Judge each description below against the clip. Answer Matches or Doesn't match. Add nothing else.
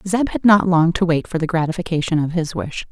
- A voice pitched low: Doesn't match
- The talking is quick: Matches